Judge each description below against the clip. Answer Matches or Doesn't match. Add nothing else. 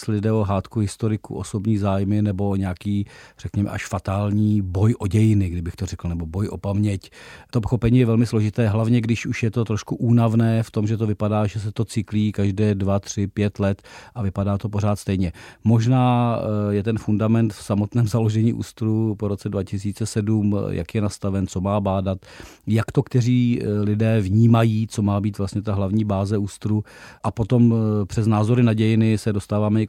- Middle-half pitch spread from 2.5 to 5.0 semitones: Doesn't match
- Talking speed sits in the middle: Doesn't match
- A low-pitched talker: Matches